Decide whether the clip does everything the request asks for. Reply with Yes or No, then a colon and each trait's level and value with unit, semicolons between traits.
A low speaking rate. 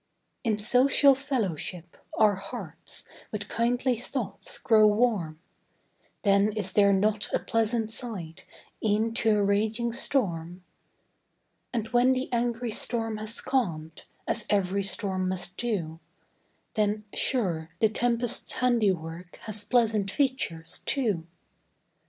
Yes: slow, 115 wpm